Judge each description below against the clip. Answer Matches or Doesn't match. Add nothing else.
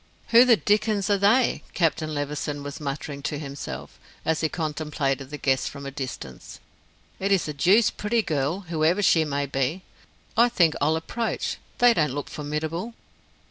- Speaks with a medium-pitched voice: Matches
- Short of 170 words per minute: Matches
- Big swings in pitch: Matches